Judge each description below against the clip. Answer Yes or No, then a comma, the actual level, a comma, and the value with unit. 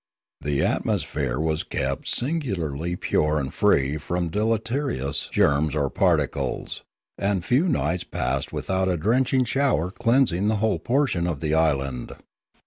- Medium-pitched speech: No, very low, 90 Hz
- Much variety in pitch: Yes, wide, 7.5 semitones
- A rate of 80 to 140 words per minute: Yes, slow, 135 wpm